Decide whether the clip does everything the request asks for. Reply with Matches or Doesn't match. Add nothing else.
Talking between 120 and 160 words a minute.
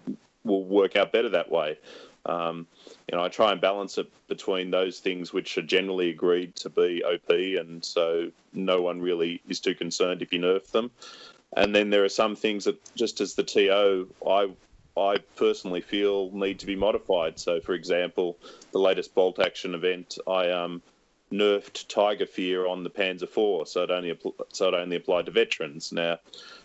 Doesn't match